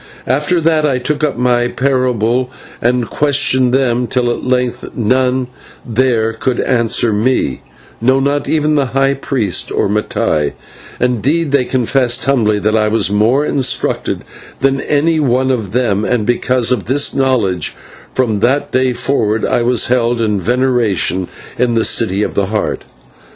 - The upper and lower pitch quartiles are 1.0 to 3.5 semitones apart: Yes, average, 2.9 semitones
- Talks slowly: No, average, 155 wpm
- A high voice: No, low, 125 Hz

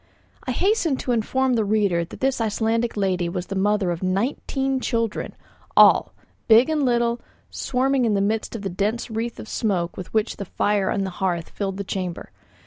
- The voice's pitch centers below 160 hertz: No, high, 215 Hz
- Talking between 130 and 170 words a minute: No, average, 190 wpm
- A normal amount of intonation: Yes, average, 3.7 semitones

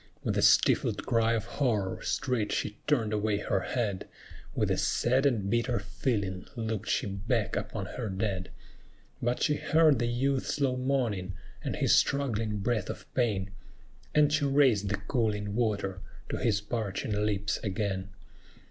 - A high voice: No, low, 110 Hz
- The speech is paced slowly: No, average, 155 wpm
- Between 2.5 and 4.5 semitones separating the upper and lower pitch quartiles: Yes, average, 3.7 semitones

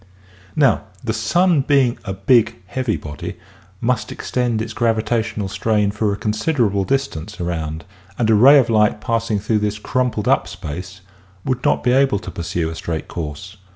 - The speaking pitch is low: Yes, low, 110 Hz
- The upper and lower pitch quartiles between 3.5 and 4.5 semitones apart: Yes, average, 4.2 semitones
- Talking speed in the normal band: Yes, average, 165 wpm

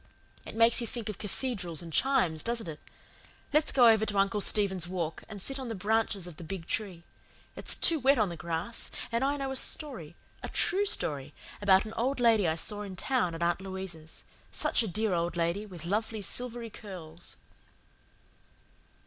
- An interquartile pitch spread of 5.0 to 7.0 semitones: Yes, average, 5.3 semitones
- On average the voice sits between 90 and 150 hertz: No, high, 205 Hz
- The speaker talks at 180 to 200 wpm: Yes, average, 190 wpm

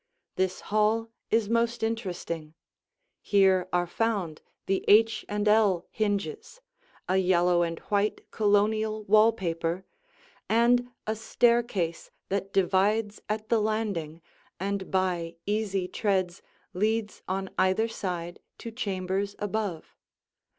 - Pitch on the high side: Yes, high, 200 Hz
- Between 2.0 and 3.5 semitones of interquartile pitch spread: Yes, average, 3.0 semitones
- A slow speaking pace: Yes, slow, 115 wpm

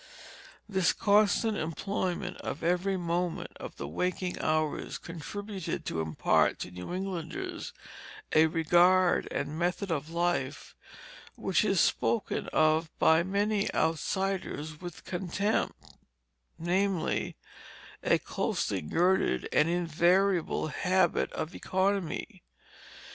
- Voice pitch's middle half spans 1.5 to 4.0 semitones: Yes, average, 3.2 semitones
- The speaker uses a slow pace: Yes, slow, 105 wpm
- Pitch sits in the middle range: Yes, medium, 175 Hz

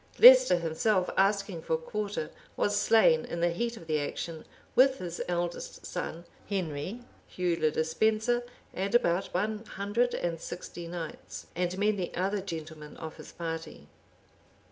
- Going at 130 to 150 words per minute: Yes, average, 145 wpm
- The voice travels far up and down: No, average, 4.3 semitones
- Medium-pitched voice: Yes, medium, 180 Hz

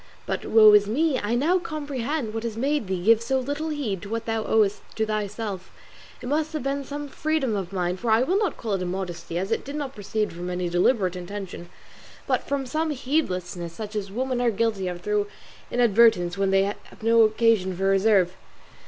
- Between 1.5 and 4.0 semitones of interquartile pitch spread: No, wide, 5.4 semitones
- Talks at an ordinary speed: No, fast, 210 wpm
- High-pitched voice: Yes, high, 220 Hz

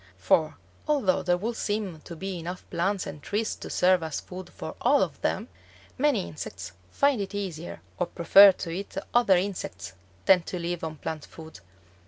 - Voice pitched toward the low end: No, medium, 185 Hz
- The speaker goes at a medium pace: Yes, average, 180 wpm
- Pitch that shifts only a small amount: No, average, 3.4 semitones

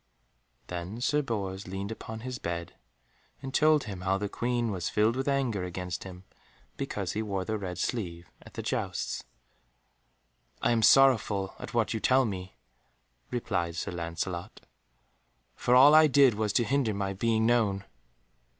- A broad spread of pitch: No, average, 4.6 semitones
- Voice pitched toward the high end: No, low, 105 Hz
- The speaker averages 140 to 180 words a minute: Yes, average, 160 wpm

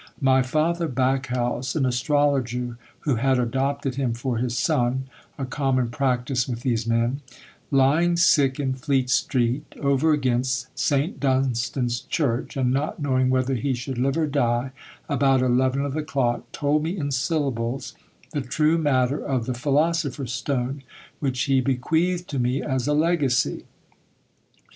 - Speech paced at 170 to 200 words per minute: No, average, 150 wpm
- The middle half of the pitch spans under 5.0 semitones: Yes, narrow, 2.4 semitones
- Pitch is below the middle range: Yes, low, 130 Hz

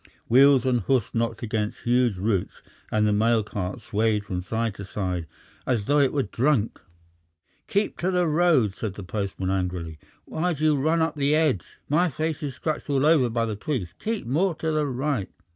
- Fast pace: No, average, 195 wpm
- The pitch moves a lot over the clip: Yes, wide, 6.5 semitones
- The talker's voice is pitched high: No, low, 120 Hz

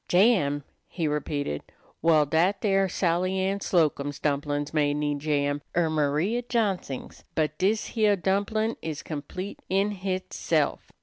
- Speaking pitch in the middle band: Yes, medium, 165 Hz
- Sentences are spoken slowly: Yes, slow, 130 wpm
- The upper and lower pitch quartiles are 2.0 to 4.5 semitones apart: No, average, 4.9 semitones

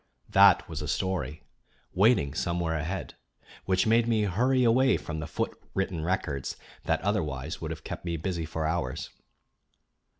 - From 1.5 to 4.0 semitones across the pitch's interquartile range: No, average, 4.4 semitones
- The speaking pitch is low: Yes, very low, 85 Hz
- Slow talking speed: No, average, 155 wpm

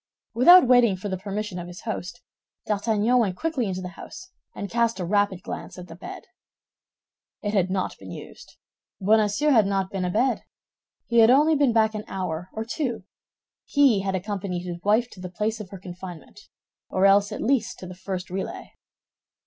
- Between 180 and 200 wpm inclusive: Yes, average, 185 wpm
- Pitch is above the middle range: Yes, high, 205 Hz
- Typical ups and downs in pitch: Yes, average, 3.7 semitones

